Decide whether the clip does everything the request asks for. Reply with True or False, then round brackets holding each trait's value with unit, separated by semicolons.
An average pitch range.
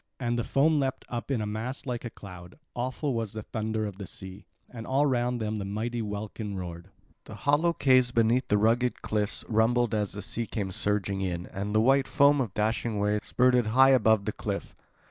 True (3.3 semitones)